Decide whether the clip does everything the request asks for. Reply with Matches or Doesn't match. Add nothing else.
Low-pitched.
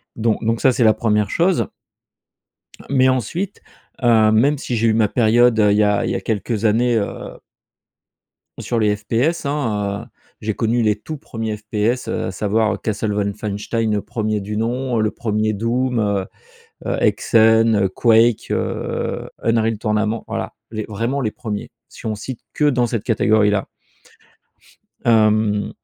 Matches